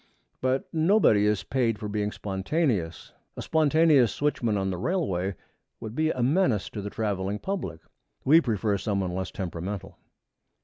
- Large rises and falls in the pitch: Yes, wide, 7.1 semitones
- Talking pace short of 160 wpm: Yes, average, 150 wpm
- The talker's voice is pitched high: No, low, 105 Hz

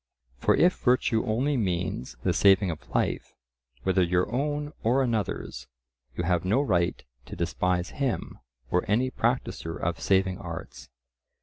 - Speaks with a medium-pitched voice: No, very low, 95 Hz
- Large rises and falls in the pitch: Yes, wide, 6.0 semitones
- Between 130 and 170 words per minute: Yes, average, 140 wpm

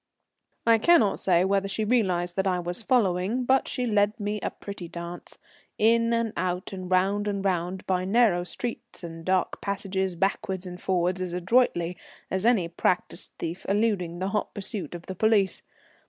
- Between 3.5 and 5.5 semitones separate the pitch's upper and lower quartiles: No, average, 2.9 semitones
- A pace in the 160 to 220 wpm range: Yes, average, 170 wpm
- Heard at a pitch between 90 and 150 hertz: No, high, 190 Hz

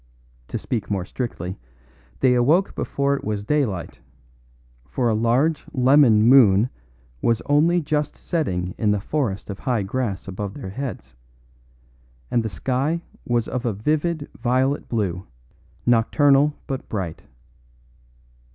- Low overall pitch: Yes, low, 120 Hz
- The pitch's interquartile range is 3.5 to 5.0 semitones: No, wide, 5.5 semitones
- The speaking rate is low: Yes, slow, 130 wpm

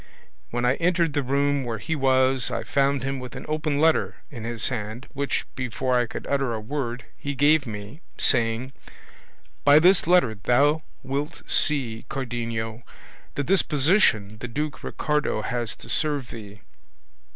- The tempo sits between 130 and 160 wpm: Yes, average, 155 wpm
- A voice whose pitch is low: Yes, low, 130 Hz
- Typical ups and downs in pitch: Yes, average, 3.9 semitones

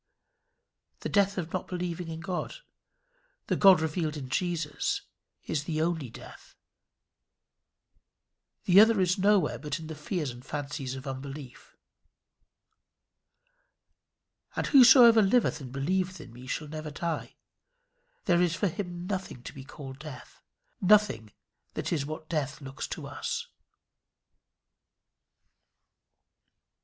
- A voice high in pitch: No, medium, 160 Hz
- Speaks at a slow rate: Yes, slow, 125 wpm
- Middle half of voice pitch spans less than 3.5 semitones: No, average, 4.7 semitones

